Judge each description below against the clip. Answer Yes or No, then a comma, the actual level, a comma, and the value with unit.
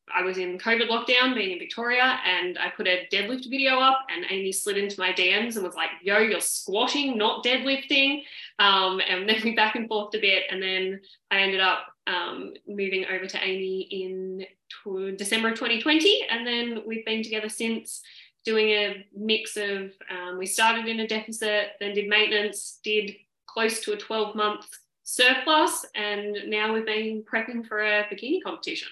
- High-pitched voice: Yes, high, 215 Hz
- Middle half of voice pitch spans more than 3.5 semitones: No, average, 2.9 semitones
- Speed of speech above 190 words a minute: No, average, 185 wpm